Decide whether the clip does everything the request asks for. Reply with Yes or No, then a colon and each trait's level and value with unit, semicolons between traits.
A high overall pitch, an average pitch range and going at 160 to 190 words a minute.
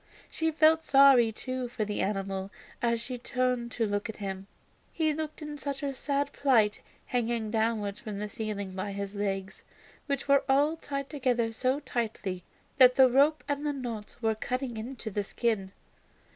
Yes: high, 240 Hz; average, 4.9 semitones; average, 170 wpm